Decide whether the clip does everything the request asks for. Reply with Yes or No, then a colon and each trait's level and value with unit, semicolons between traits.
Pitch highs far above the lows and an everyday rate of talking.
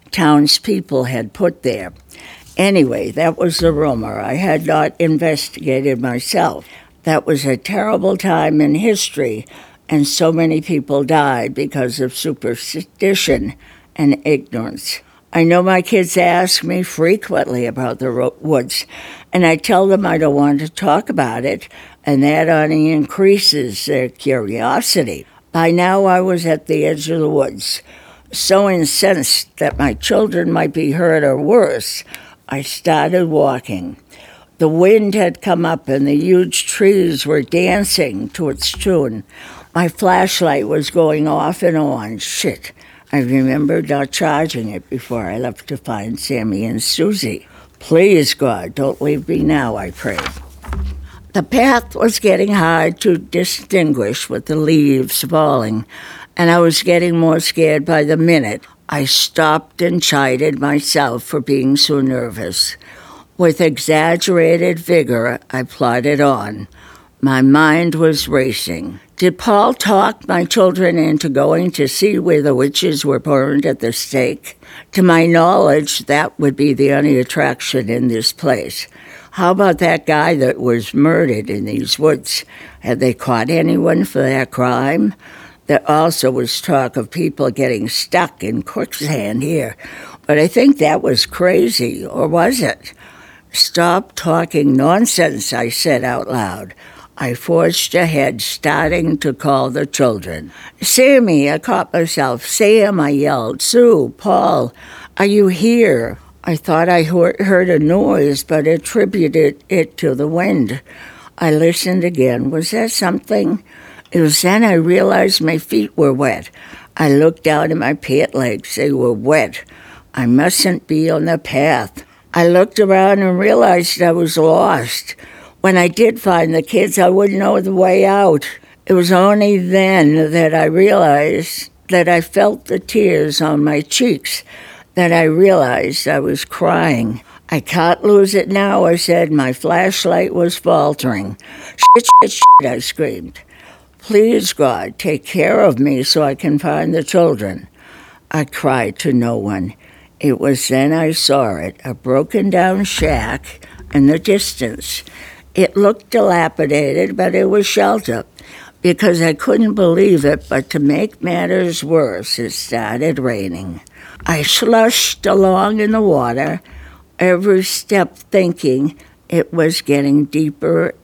No: average, 4.5 semitones; average, 150 wpm